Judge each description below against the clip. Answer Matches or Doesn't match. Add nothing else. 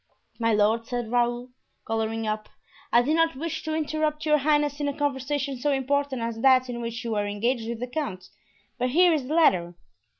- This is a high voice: Matches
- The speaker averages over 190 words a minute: Matches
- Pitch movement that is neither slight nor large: Matches